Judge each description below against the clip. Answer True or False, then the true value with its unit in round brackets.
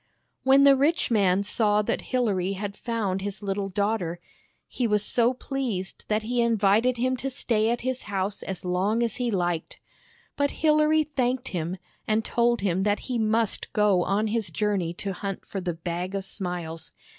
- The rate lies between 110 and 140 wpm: False (180 wpm)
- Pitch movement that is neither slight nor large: True (4.0 semitones)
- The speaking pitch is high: True (210 Hz)